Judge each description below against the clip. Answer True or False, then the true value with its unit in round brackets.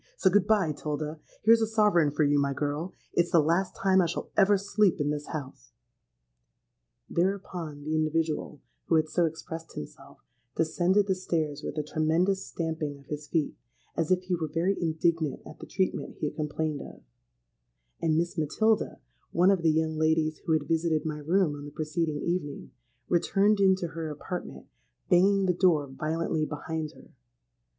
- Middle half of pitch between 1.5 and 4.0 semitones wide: True (3.2 semitones)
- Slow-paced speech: False (170 wpm)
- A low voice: False (160 Hz)